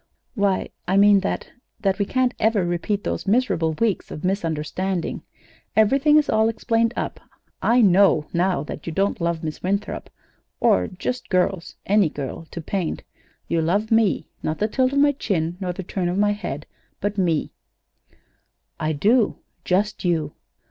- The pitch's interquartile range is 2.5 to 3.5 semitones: No, average, 4.1 semitones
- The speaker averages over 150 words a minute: Yes, average, 160 wpm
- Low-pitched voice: No, high, 195 Hz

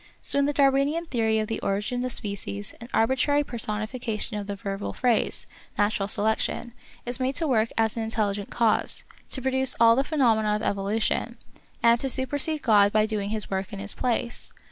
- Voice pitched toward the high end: Yes, high, 225 Hz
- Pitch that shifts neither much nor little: Yes, average, 3.6 semitones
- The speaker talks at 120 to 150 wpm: No, average, 185 wpm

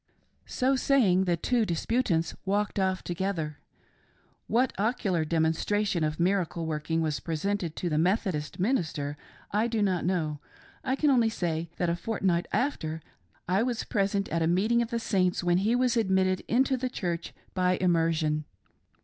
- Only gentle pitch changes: No, average, 5.0 semitones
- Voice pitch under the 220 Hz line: Yes, medium, 185 Hz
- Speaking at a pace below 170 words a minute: Yes, average, 160 wpm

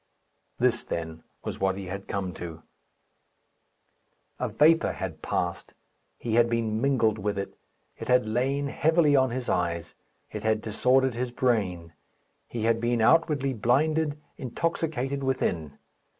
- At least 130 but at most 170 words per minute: Yes, slow, 135 wpm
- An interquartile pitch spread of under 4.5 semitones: No, wide, 5.5 semitones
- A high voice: No, low, 120 Hz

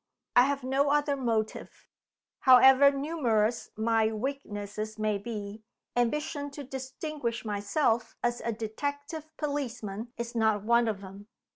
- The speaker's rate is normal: No, slow, 125 wpm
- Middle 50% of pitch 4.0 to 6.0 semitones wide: Yes, average, 4.5 semitones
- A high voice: Yes, high, 235 Hz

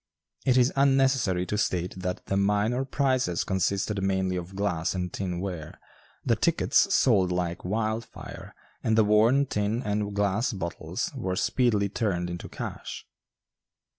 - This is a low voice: Yes, low, 100 Hz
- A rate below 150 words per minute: Yes, average, 140 wpm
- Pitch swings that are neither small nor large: Yes, average, 3.7 semitones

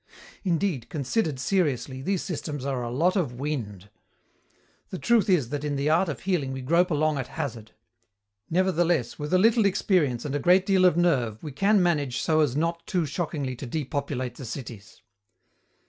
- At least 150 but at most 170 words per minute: No, average, 180 wpm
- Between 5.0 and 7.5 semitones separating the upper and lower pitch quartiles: Yes, average, 5.3 semitones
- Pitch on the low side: No, medium, 150 Hz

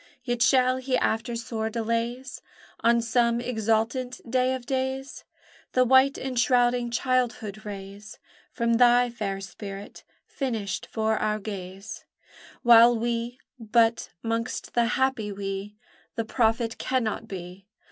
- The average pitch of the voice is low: No, high, 230 Hz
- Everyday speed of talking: No, slow, 120 wpm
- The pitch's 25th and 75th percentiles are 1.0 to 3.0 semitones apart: Yes, narrow, 2.4 semitones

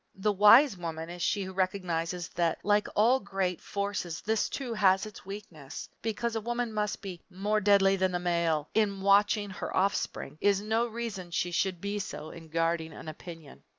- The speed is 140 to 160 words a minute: No, average, 185 wpm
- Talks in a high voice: Yes, high, 195 Hz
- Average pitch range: Yes, average, 3.3 semitones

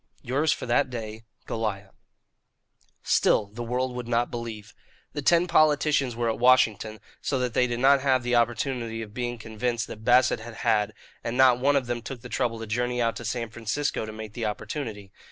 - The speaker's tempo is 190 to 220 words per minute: Yes, average, 195 wpm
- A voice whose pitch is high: No, low, 120 Hz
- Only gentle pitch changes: Yes, narrow, 2.3 semitones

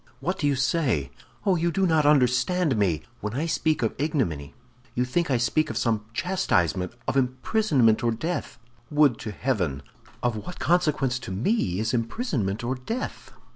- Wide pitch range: Yes, wide, 6.5 semitones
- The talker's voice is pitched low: Yes, low, 130 Hz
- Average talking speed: Yes, average, 170 wpm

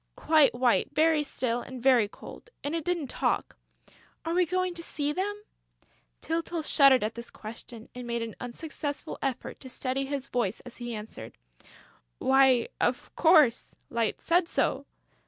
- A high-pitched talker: Yes, very high, 270 Hz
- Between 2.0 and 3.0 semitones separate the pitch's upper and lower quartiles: No, average, 5.3 semitones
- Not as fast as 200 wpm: Yes, average, 155 wpm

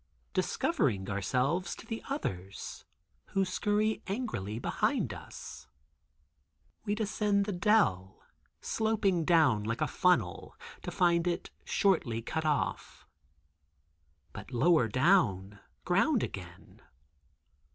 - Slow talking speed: Yes, slow, 100 wpm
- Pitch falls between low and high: Yes, medium, 170 Hz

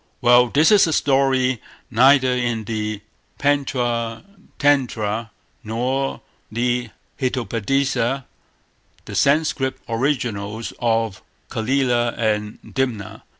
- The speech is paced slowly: Yes, slow, 90 wpm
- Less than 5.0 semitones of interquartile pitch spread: Yes, average, 3.0 semitones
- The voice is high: No, low, 120 Hz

